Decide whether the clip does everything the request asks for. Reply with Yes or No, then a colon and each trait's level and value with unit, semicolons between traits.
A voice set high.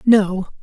Yes: high, 200 Hz